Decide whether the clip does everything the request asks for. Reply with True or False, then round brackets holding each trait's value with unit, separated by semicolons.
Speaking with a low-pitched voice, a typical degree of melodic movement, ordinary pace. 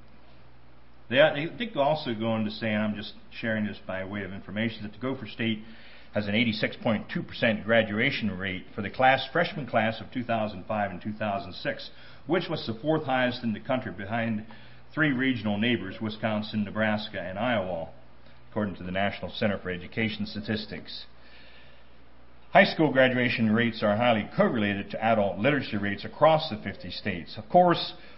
True (110 Hz; 3.4 semitones; 160 wpm)